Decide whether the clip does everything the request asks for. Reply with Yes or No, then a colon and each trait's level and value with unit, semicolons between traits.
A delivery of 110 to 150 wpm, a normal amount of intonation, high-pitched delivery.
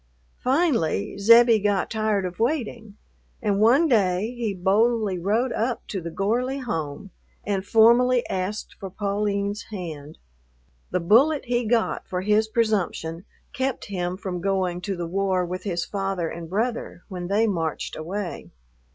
Yes: average, 145 wpm; average, 3.9 semitones; high, 200 Hz